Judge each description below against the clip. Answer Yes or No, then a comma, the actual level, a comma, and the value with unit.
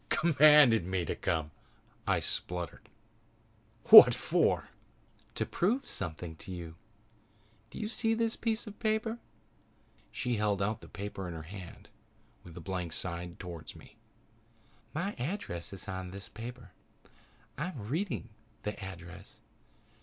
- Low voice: Yes, low, 100 Hz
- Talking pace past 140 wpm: No, slow, 135 wpm